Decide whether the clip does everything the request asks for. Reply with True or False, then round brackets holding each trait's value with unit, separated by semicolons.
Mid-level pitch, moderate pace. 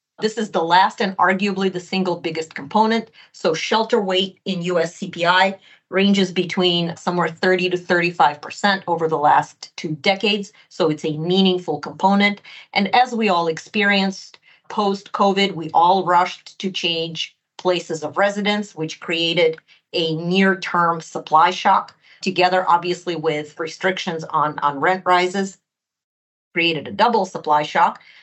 True (180 Hz; 145 wpm)